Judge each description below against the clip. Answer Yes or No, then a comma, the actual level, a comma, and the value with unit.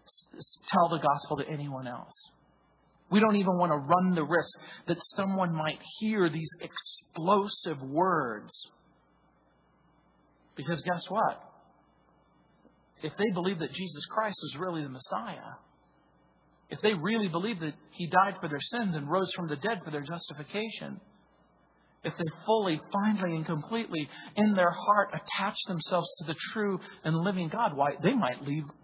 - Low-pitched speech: No, medium, 175 Hz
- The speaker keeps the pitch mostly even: No, average, 4.2 semitones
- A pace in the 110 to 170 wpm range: Yes, average, 150 wpm